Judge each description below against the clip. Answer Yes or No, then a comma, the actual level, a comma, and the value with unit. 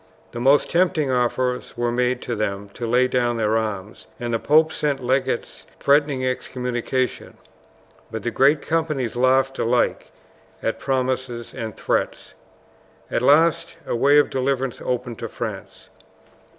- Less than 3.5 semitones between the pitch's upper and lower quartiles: Yes, narrow, 2.4 semitones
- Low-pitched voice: Yes, low, 125 Hz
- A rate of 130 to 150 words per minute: Yes, average, 140 wpm